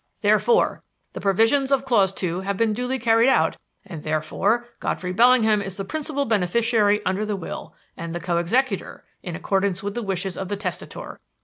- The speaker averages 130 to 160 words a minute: No, average, 180 wpm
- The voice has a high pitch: Yes, high, 205 Hz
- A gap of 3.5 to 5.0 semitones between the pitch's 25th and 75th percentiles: Yes, average, 4.1 semitones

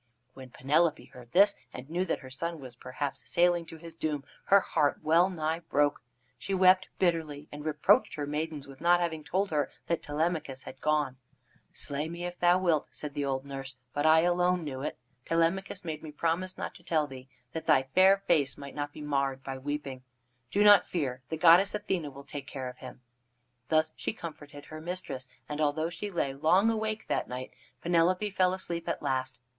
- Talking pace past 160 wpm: Yes, average, 195 wpm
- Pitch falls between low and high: Yes, medium, 155 Hz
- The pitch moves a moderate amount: Yes, average, 3.8 semitones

